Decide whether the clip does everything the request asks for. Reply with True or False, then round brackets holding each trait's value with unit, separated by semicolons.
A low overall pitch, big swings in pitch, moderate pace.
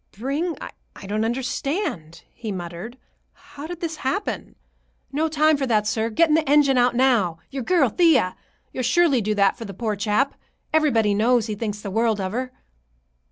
False (245 Hz; 5.7 semitones; 170 wpm)